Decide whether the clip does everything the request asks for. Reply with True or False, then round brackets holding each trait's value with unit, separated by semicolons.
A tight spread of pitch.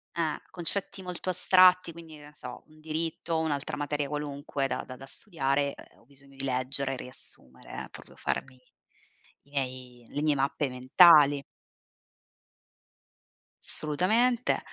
False (3.4 semitones)